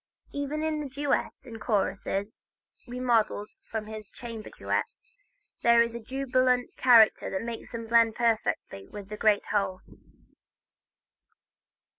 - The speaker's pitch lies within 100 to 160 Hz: No, high, 230 Hz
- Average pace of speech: No, slow, 125 wpm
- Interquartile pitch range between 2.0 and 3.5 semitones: Yes, average, 2.8 semitones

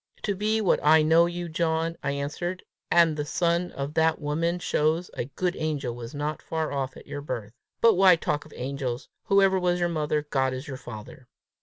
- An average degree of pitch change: Yes, average, 3.6 semitones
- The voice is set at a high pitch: No, medium, 155 Hz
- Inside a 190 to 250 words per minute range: Yes, average, 200 wpm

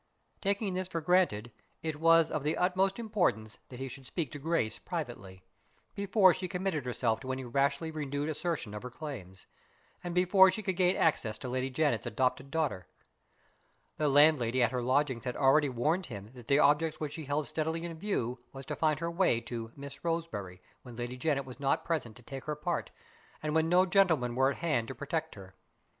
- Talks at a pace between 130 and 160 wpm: No, average, 200 wpm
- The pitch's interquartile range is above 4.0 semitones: Yes, average, 5.1 semitones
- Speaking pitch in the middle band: Yes, medium, 145 Hz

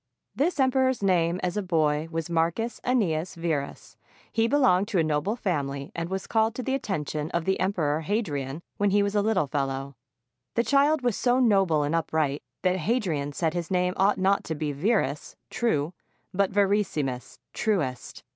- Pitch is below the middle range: No, medium, 180 Hz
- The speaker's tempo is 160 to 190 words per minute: Yes, average, 175 wpm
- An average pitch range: No, wide, 5.7 semitones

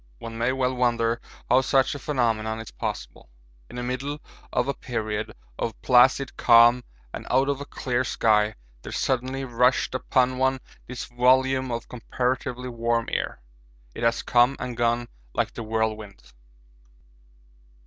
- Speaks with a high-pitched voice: No, low, 125 Hz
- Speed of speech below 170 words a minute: Yes, average, 150 wpm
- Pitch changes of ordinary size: No, narrow, 2.0 semitones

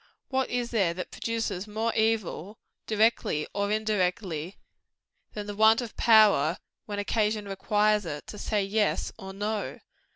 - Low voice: No, high, 210 Hz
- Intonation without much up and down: Yes, narrow, 2.0 semitones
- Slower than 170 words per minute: Yes, average, 150 wpm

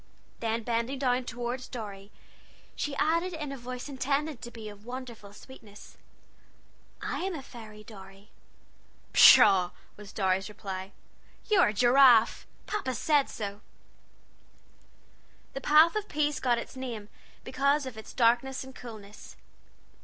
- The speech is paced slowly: Yes, slow, 130 wpm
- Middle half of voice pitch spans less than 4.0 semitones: No, average, 4.5 semitones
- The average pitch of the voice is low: No, high, 240 Hz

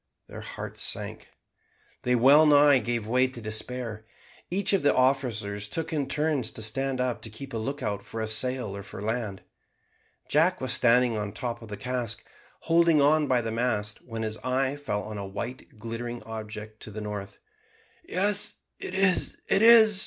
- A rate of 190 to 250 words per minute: No, average, 180 wpm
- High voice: No, low, 125 Hz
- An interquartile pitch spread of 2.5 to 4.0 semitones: No, average, 4.7 semitones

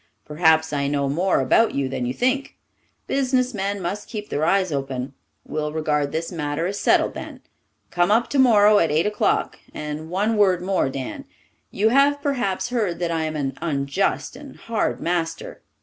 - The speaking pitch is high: No, medium, 175 Hz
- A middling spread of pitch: No, wide, 6.3 semitones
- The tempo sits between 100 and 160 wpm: No, average, 170 wpm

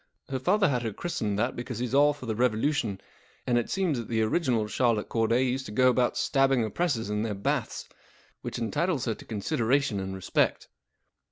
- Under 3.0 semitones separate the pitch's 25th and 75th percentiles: No, average, 3.6 semitones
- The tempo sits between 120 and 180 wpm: No, average, 190 wpm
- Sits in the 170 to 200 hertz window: No, low, 120 Hz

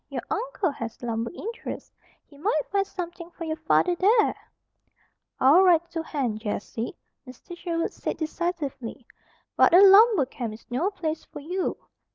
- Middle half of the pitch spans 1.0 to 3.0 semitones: No, wide, 5.6 semitones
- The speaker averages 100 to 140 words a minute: No, average, 155 wpm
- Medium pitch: No, very high, 330 Hz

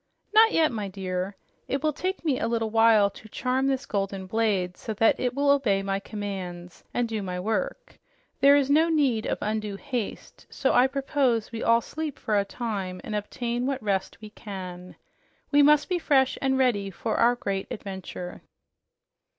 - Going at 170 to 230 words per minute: Yes, average, 185 wpm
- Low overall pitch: No, high, 225 Hz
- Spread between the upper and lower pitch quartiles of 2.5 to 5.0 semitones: No, wide, 5.5 semitones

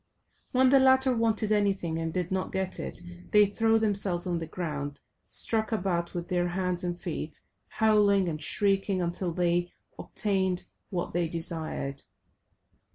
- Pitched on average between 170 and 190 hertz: Yes, medium, 185 Hz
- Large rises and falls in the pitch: No, average, 3.3 semitones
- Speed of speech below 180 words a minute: Yes, average, 150 wpm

